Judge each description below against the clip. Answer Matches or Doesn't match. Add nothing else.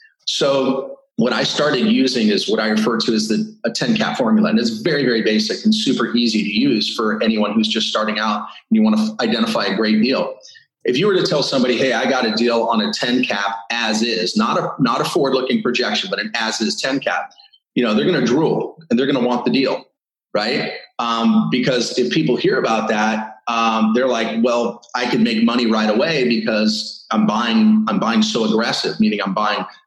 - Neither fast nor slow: Doesn't match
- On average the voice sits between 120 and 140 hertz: Matches